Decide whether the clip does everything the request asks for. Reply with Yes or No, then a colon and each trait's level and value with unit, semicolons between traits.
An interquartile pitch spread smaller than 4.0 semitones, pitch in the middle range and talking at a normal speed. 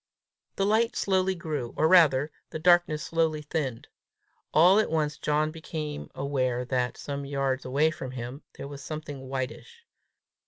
Yes: average, 3.3 semitones; medium, 150 Hz; average, 150 wpm